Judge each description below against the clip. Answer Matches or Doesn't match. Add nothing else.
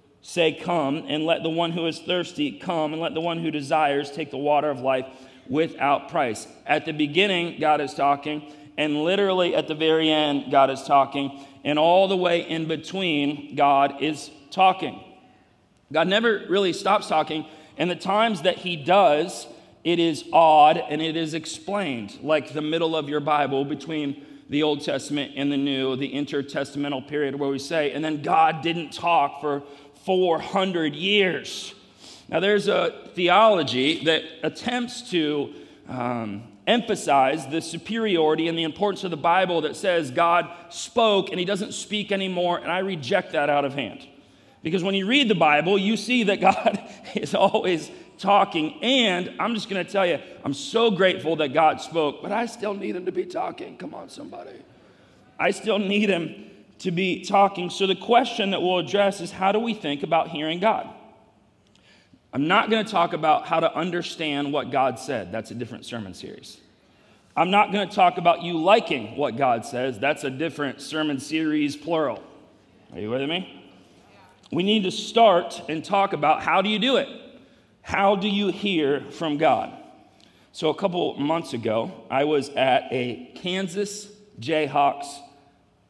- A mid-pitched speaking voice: Matches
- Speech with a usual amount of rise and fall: Matches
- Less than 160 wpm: Doesn't match